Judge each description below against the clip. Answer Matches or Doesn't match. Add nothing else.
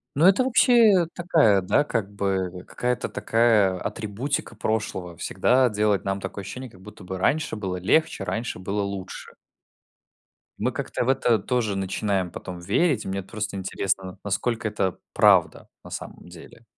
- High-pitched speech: Doesn't match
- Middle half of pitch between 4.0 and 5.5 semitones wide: Matches